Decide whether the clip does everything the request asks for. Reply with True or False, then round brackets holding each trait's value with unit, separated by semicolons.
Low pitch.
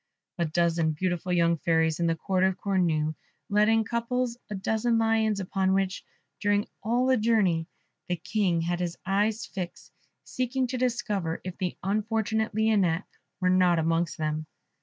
False (190 Hz)